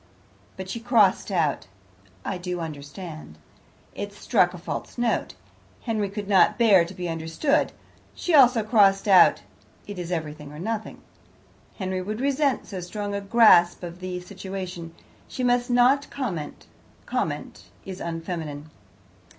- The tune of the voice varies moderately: Yes, average, 4.6 semitones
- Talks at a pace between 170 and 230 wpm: No, average, 140 wpm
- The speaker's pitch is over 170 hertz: Yes, high, 190 Hz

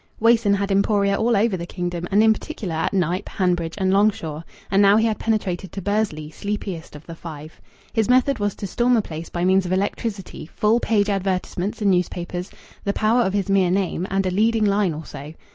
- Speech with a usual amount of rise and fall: Yes, average, 3.1 semitones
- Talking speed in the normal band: No, fast, 210 wpm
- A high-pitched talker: Yes, high, 195 Hz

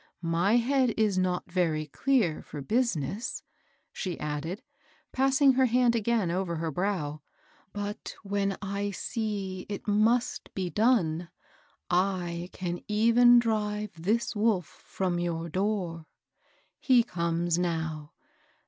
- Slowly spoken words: Yes, slow, 120 wpm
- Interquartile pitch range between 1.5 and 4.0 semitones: No, average, 4.9 semitones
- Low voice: No, high, 195 Hz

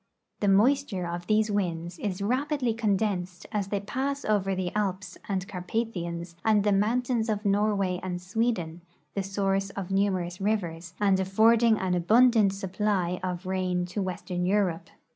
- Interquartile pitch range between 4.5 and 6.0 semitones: No, average, 2.9 semitones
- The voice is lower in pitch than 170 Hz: No, high, 195 Hz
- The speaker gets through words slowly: No, average, 150 wpm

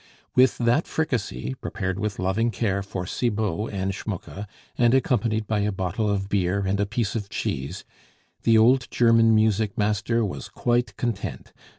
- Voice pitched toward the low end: Yes, low, 105 Hz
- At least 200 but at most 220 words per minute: No, average, 160 wpm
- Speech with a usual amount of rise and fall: Yes, average, 3.0 semitones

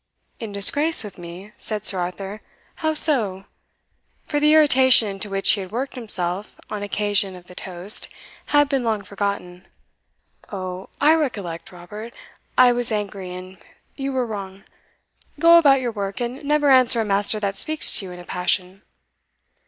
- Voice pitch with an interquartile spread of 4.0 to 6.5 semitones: Yes, average, 5.2 semitones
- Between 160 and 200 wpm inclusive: Yes, average, 165 wpm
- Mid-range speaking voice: No, high, 205 Hz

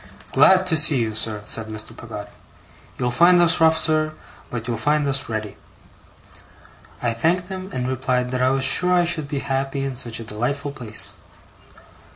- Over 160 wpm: Yes, average, 180 wpm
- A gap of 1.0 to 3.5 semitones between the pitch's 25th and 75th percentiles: No, average, 5.2 semitones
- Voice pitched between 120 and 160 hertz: Yes, low, 135 Hz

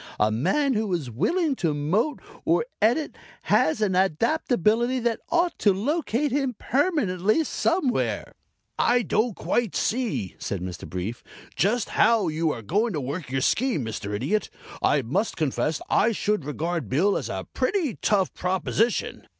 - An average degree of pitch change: No, wide, 8.5 semitones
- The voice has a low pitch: No, high, 210 Hz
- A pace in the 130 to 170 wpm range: Yes, average, 150 wpm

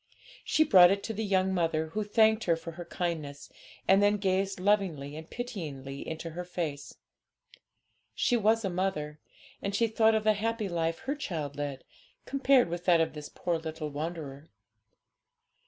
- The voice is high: No, medium, 175 Hz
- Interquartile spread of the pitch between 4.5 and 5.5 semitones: Yes, average, 4.9 semitones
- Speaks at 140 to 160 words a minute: No, average, 170 wpm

